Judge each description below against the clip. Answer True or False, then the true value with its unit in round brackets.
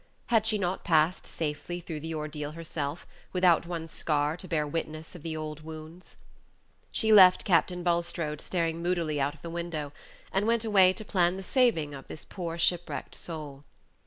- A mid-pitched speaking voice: True (165 Hz)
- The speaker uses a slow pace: False (175 wpm)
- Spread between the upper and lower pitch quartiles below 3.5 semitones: True (2.8 semitones)